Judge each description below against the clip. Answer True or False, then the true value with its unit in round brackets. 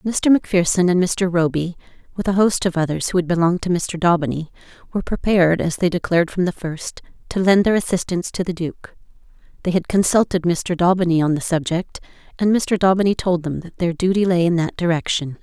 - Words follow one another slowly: False (200 wpm)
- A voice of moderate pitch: True (175 Hz)